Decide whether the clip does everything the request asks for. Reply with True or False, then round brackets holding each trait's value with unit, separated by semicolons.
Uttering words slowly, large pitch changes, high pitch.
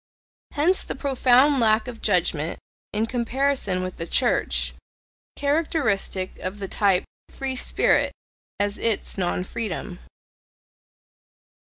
True (110 wpm; 6.3 semitones; 215 Hz)